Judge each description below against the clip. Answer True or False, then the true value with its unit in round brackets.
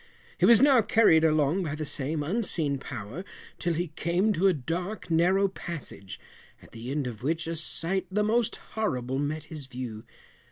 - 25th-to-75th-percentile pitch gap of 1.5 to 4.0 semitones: False (5.3 semitones)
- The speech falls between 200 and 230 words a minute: False (175 wpm)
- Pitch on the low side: False (160 Hz)